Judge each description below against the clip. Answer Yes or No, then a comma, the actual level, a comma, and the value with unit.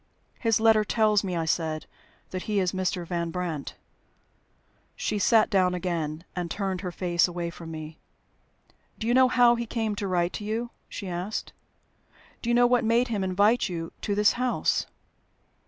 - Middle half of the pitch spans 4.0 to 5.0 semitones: Yes, average, 4.3 semitones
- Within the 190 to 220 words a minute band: No, average, 175 wpm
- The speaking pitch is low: No, high, 190 Hz